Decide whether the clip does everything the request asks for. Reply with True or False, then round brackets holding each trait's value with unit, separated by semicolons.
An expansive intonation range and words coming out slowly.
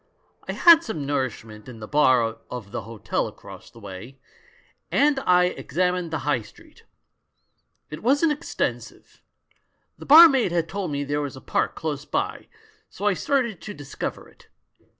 False (8.3 semitones; 160 wpm)